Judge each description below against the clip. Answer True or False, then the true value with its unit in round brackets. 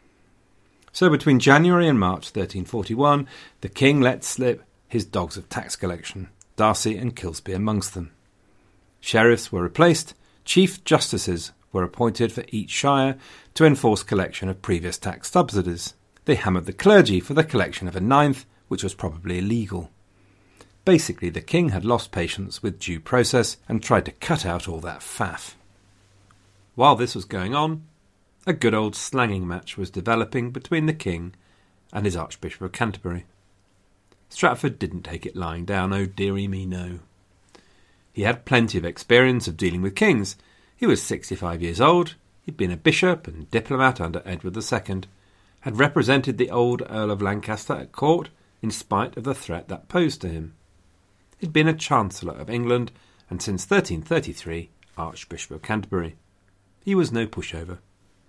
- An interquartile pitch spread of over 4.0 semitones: True (5.1 semitones)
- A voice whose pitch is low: True (100 Hz)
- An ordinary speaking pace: True (160 wpm)